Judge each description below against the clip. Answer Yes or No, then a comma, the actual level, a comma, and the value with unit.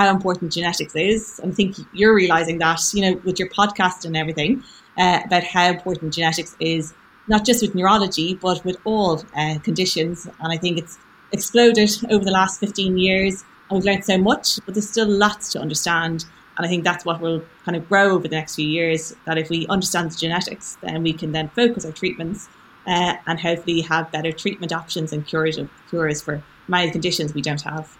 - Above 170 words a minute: Yes, fast, 205 wpm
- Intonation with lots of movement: No, average, 3.1 semitones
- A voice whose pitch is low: No, medium, 175 Hz